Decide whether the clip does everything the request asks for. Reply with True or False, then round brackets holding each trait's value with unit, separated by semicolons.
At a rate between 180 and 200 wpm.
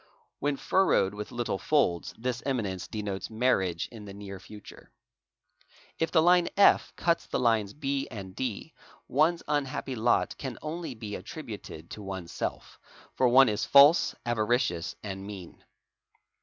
False (140 wpm)